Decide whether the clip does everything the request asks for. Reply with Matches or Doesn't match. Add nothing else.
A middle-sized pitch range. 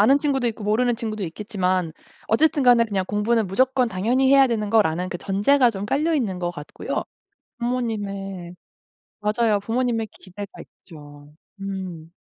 Matches